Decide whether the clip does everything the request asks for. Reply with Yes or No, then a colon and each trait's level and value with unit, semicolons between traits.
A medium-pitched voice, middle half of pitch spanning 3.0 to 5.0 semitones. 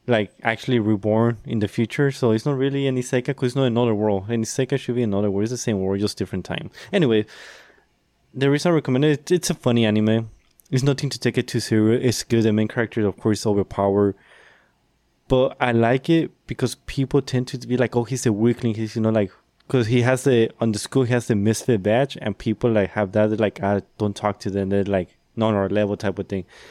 No: low, 115 Hz; average, 3.5 semitones